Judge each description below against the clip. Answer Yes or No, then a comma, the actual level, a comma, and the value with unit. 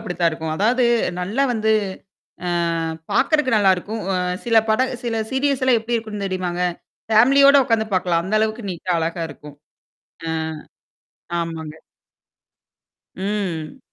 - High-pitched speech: Yes, high, 210 Hz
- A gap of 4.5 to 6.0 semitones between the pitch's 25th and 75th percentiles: Yes, average, 4.8 semitones